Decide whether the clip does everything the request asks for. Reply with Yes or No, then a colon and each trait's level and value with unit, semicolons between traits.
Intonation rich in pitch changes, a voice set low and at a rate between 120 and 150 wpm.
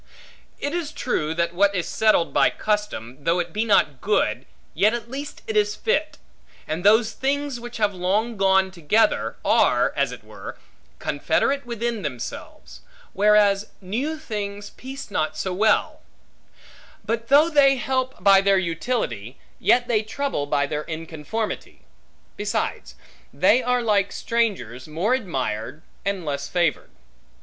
No: wide, 5.9 semitones; high, 205 Hz; average, 140 wpm